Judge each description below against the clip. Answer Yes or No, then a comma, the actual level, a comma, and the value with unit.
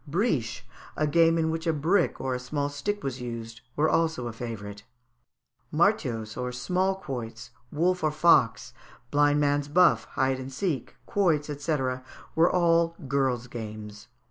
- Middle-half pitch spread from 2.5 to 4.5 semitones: No, average, 5.2 semitones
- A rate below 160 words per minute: Yes, average, 150 wpm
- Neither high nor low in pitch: Yes, medium, 145 Hz